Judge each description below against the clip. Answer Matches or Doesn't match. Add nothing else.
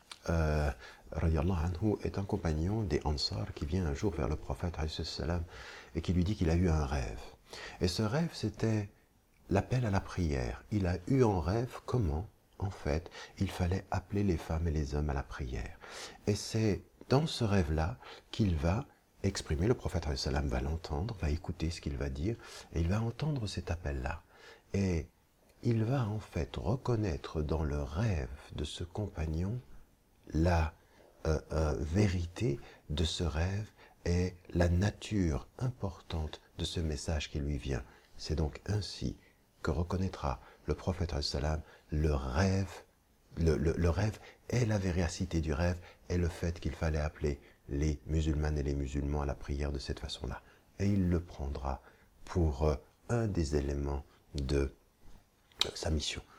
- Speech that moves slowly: Doesn't match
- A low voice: Matches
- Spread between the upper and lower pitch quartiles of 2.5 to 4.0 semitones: Doesn't match